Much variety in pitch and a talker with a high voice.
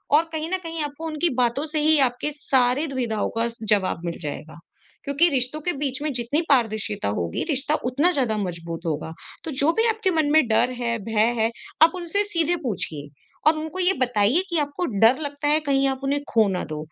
Yes: wide, 5.9 semitones; very high, 275 Hz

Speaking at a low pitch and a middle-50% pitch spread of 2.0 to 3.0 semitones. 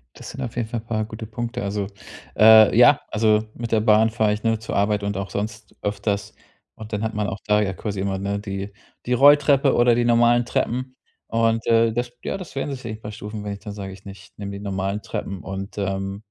Yes: low, 110 Hz; narrow, 2.5 semitones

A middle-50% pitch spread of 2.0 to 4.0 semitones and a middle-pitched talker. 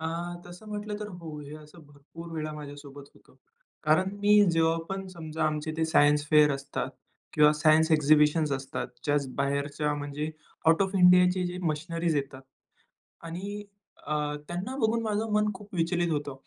Yes: average, 3.5 semitones; medium, 160 Hz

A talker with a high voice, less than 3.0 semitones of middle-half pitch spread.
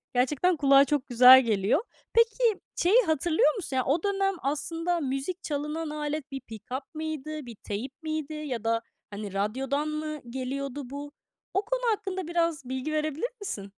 No: very high, 295 Hz; average, 4.1 semitones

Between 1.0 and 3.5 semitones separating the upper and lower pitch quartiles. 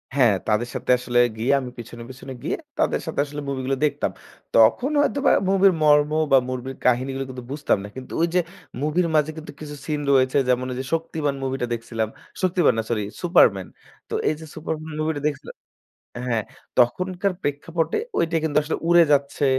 No: average, 4.2 semitones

